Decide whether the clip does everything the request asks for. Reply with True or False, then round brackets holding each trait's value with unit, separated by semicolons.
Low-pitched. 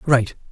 True (130 Hz)